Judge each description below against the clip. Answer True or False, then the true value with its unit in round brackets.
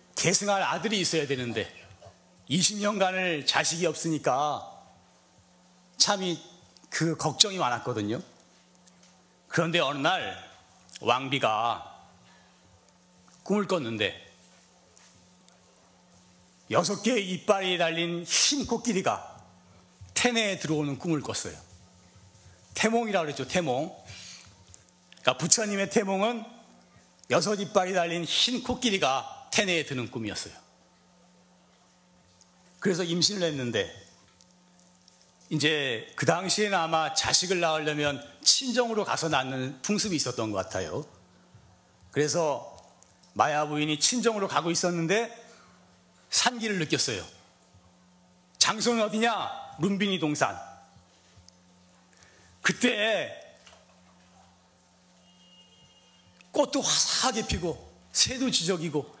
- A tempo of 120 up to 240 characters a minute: True (215 characters per minute)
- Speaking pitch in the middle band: True (160 Hz)